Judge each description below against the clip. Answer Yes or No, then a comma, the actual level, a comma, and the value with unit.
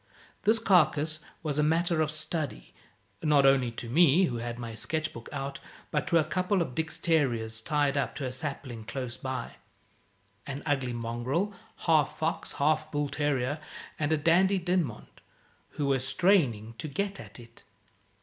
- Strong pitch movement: No, average, 4.2 semitones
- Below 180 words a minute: Yes, average, 165 wpm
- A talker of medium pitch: Yes, medium, 145 Hz